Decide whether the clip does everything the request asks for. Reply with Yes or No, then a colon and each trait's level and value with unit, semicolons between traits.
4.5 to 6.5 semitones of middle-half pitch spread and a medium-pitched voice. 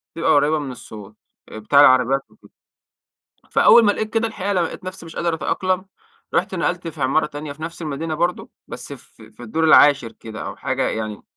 Yes: wide, 5.4 semitones; medium, 155 Hz